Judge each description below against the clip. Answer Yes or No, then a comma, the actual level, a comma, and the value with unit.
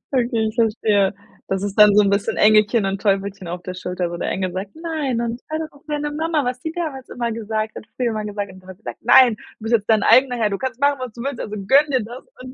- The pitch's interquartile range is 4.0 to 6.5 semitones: Yes, average, 4.3 semitones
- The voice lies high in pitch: Yes, high, 225 Hz